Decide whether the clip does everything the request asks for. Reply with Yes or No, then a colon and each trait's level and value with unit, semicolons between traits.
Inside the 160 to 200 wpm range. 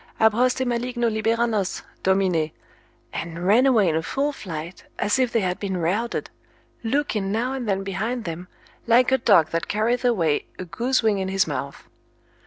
Yes: average, 180 wpm